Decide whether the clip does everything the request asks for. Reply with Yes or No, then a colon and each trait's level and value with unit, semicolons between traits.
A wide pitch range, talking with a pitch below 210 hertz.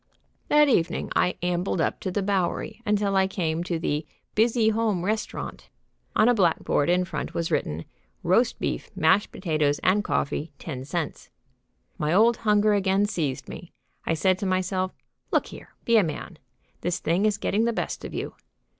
No: average, 4.2 semitones; medium, 185 Hz